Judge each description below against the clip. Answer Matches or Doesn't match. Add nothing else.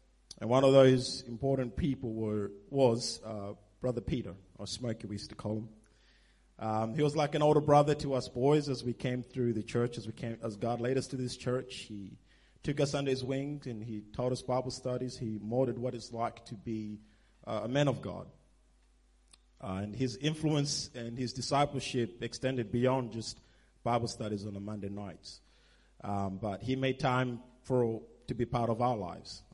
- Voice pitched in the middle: Doesn't match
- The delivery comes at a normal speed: Matches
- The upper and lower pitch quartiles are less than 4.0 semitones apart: Matches